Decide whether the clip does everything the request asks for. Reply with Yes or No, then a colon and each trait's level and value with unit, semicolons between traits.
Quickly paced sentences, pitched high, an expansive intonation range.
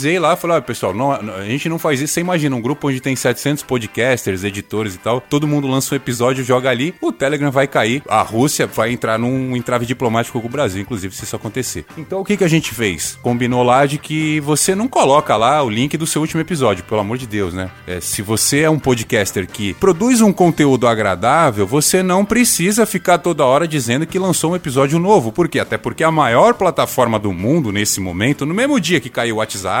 No: fast, 230 wpm; low, 135 Hz; wide, 5.9 semitones